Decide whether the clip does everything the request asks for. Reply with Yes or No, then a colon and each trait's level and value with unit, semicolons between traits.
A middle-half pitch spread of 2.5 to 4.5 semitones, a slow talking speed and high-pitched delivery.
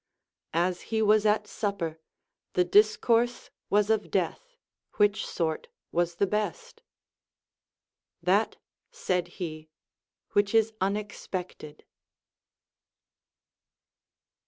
Yes: average, 3.5 semitones; slow, 85 wpm; high, 205 Hz